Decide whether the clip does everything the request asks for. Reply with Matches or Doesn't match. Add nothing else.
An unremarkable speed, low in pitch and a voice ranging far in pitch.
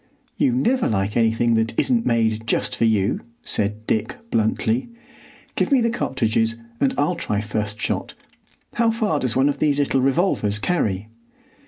Matches